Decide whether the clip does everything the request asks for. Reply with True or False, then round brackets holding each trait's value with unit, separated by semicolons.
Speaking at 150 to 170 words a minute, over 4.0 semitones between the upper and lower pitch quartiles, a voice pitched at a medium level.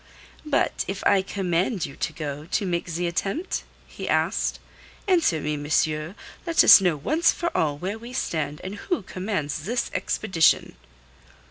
True (155 wpm; 5.6 semitones; 180 Hz)